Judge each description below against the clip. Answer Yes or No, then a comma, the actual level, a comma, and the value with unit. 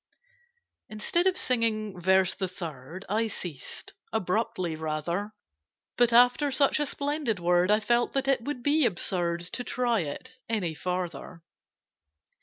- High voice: Yes, high, 210 Hz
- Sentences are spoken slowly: Yes, slow, 130 wpm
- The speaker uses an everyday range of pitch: No, wide, 5.8 semitones